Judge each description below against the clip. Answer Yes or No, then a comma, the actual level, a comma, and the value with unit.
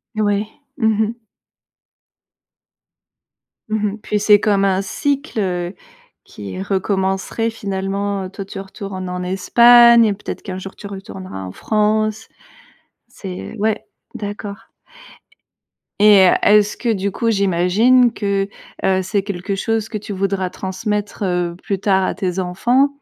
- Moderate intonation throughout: No, narrow, 2.2 semitones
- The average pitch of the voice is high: Yes, high, 200 Hz